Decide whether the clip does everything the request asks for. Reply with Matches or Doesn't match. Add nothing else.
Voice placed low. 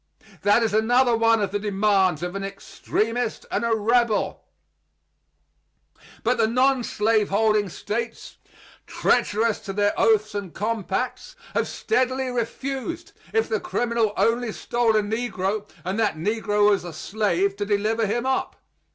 Doesn't match